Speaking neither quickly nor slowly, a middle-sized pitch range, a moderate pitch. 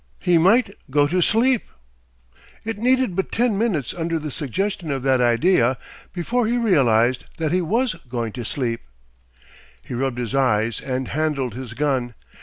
No: average, 160 wpm; wide, 7.7 semitones; medium, 150 Hz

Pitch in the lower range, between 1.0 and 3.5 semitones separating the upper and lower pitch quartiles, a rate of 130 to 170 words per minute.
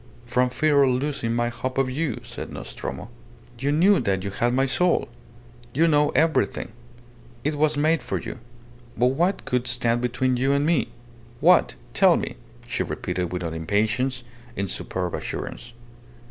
No: low, 125 Hz; average, 4.1 semitones; average, 160 wpm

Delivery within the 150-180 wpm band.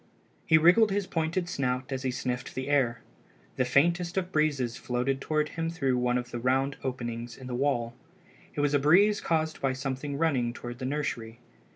No: average, 190 wpm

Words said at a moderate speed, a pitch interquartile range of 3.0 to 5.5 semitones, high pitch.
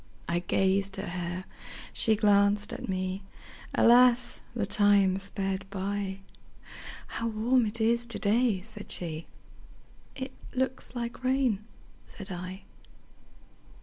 No: slow, 105 wpm; average, 3.5 semitones; high, 205 Hz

